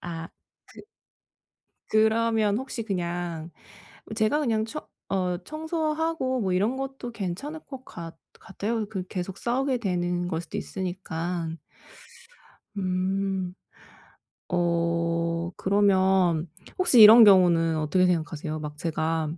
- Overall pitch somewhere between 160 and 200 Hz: Yes, medium, 185 Hz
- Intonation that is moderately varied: Yes, average, 4.9 semitones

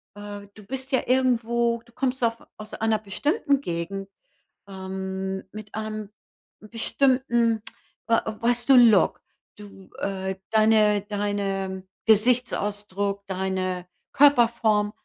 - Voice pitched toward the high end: Yes, high, 215 Hz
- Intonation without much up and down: No, average, 3.2 semitones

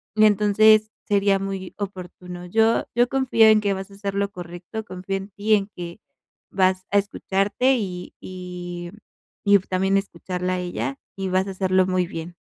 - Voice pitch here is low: No, high, 195 Hz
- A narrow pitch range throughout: Yes, narrow, 2.2 semitones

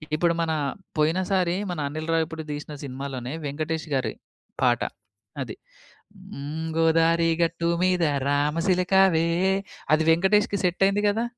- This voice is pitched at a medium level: Yes, medium, 165 Hz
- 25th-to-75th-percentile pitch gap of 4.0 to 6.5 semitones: No, average, 3.1 semitones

